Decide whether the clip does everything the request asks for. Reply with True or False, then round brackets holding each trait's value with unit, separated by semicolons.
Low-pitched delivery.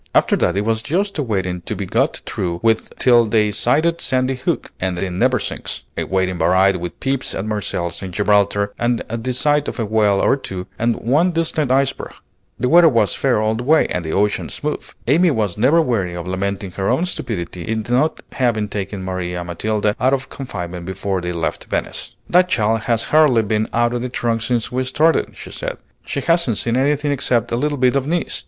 True (115 Hz)